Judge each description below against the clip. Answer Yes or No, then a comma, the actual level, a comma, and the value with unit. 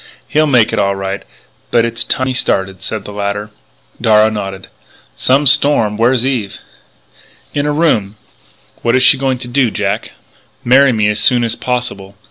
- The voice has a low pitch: Yes, low, 115 Hz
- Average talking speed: Yes, average, 175 wpm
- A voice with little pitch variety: No, average, 4.0 semitones